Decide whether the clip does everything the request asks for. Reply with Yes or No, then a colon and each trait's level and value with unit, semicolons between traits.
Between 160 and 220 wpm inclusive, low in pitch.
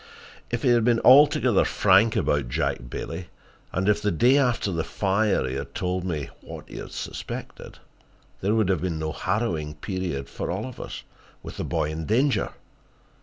Yes: average, 175 wpm; very low, 95 Hz